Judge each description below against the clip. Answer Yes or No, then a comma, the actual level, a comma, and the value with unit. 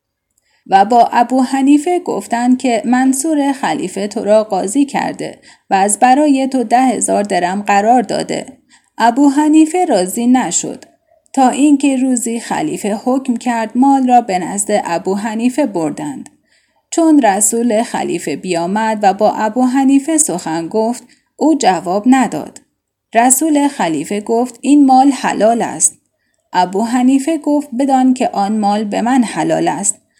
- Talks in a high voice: Yes, very high, 250 Hz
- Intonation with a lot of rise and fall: No, average, 4.4 semitones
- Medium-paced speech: Yes, average, 135 wpm